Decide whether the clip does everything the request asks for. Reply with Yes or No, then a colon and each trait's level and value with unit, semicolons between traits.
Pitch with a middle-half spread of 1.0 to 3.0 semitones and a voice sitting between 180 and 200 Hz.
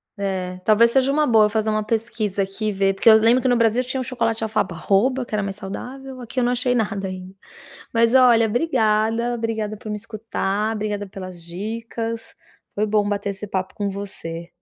No: average, 2.7 semitones; high, 215 Hz